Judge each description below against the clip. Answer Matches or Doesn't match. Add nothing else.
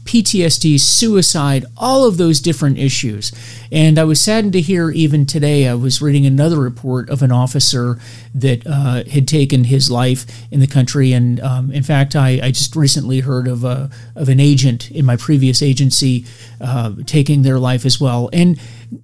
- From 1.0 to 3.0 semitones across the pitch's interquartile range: Matches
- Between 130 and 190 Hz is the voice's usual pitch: Matches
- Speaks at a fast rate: Doesn't match